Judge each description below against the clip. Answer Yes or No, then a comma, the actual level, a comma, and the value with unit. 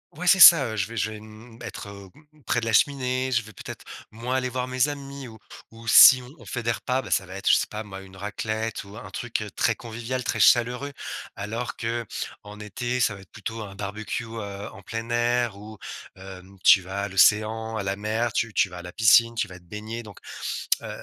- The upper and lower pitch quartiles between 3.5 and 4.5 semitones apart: No, average, 2.9 semitones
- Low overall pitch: Yes, low, 110 Hz